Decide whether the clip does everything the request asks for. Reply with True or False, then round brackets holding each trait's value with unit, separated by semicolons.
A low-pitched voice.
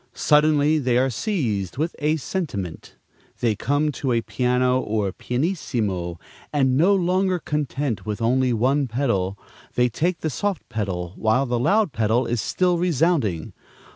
True (130 Hz)